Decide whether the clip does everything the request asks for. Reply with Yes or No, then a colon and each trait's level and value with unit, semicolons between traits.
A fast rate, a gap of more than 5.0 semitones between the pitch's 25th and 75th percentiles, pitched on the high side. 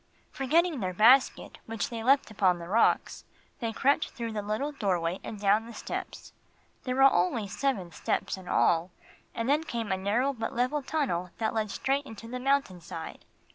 No: average, 180 wpm; wide, 5.4 semitones; high, 225 Hz